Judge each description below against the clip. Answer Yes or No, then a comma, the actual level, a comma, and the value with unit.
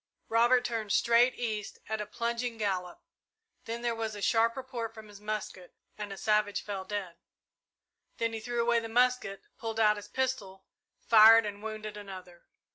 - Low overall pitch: No, high, 220 Hz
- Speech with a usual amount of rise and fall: No, narrow, 2.2 semitones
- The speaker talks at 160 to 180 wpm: Yes, average, 170 wpm